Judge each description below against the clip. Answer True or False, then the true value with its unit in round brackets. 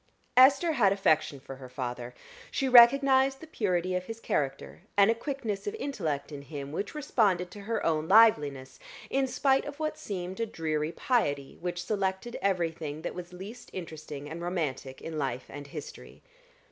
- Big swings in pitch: True (7.6 semitones)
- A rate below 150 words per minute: False (170 wpm)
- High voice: False (180 Hz)